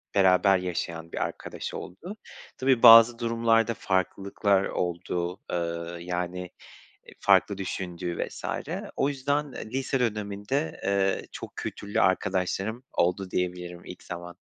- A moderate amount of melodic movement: Yes, average, 4.4 semitones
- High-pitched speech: No, very low, 95 Hz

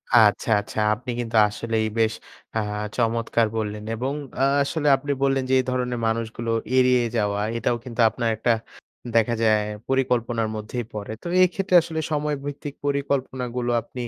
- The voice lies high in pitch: No, low, 120 Hz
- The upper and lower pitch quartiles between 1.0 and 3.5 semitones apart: Yes, average, 3.0 semitones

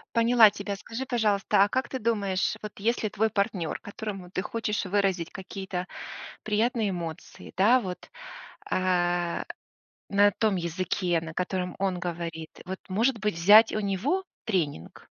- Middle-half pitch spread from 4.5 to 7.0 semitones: No, average, 3.3 semitones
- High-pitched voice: Yes, high, 195 Hz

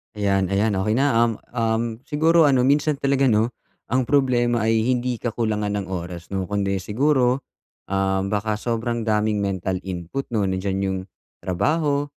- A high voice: No, low, 110 Hz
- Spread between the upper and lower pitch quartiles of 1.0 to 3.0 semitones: No, average, 4.5 semitones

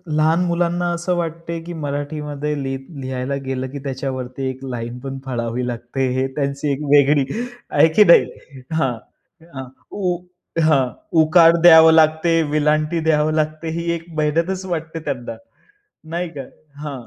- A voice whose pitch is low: No, medium, 150 Hz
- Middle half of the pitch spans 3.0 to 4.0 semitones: Yes, average, 3.6 semitones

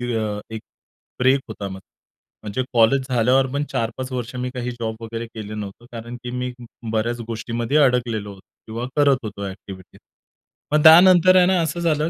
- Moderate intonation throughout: Yes, average, 3.3 semitones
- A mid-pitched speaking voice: No, low, 120 Hz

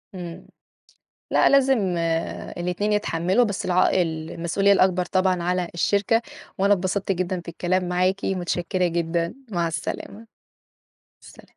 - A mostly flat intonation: Yes, narrow, 2.2 semitones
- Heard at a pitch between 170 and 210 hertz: Yes, medium, 185 Hz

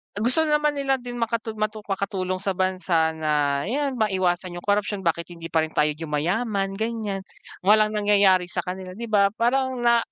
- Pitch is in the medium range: No, high, 200 Hz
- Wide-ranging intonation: No, average, 4.5 semitones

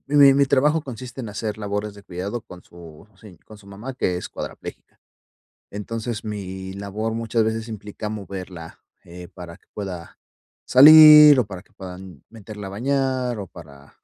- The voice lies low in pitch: Yes, low, 105 Hz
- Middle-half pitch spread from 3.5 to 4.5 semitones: Yes, average, 4.2 semitones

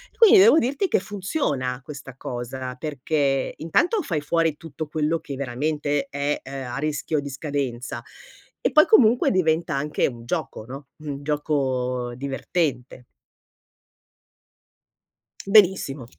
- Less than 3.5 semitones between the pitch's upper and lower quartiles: No, average, 3.8 semitones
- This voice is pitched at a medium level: Yes, medium, 145 Hz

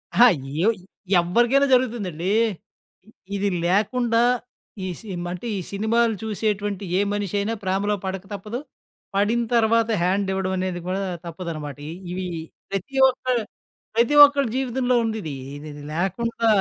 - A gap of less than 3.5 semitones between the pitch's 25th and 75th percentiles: No, average, 3.8 semitones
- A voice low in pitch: No, high, 205 Hz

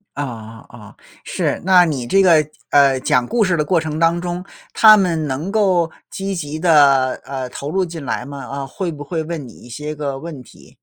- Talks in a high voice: No, medium, 155 Hz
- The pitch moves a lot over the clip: No, average, 4.4 semitones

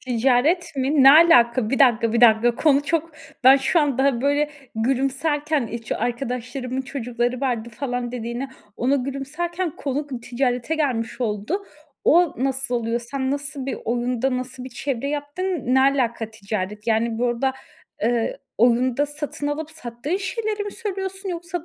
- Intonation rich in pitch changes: No, average, 3.6 semitones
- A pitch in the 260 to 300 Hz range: Yes, very high, 265 Hz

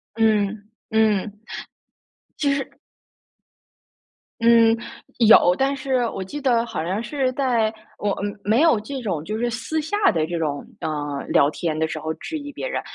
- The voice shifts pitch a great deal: Yes, wide, 6.0 semitones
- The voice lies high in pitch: Yes, high, 220 Hz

